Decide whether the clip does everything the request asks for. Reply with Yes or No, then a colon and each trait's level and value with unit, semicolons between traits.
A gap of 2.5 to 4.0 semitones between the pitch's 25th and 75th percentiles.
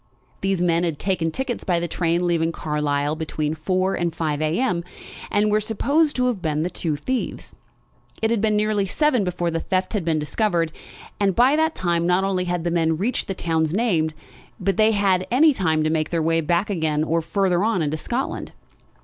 No: average, 4.5 semitones